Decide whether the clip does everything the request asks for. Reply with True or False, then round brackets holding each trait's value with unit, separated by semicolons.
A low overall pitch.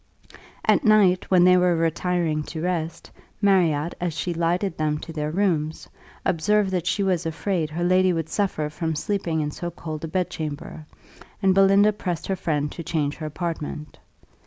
False (170 Hz)